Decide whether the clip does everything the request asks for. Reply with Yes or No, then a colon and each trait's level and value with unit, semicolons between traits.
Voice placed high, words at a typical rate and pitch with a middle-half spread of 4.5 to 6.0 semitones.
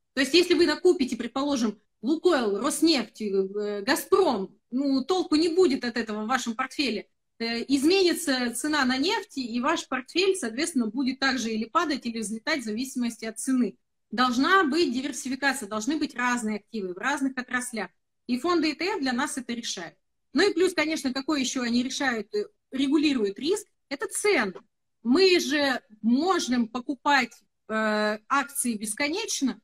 Yes: very high, 265 Hz; average, 145 wpm; average, 4.9 semitones